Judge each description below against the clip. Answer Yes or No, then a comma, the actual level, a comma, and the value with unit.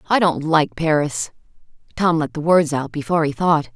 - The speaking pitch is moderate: Yes, medium, 155 Hz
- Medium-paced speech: Yes, average, 190 wpm